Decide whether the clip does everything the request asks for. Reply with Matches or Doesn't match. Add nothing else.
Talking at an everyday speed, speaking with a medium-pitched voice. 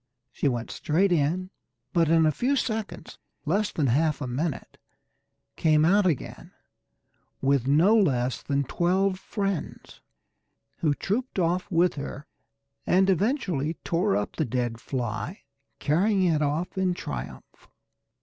Doesn't match